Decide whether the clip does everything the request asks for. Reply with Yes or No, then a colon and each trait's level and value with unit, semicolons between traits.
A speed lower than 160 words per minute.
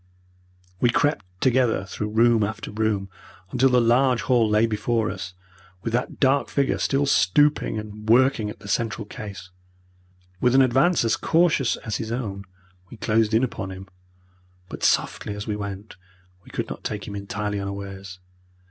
No: average, 165 wpm